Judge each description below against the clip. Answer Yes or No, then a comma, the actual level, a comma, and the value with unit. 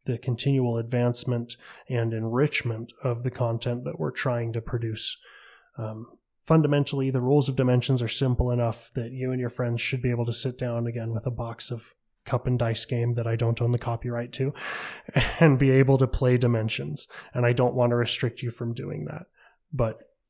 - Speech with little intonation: Yes, narrow, 1.6 semitones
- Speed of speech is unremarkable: Yes, average, 195 wpm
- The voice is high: No, low, 120 Hz